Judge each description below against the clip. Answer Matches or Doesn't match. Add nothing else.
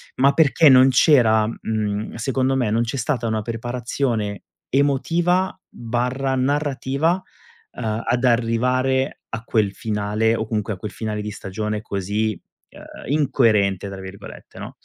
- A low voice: Matches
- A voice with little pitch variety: Doesn't match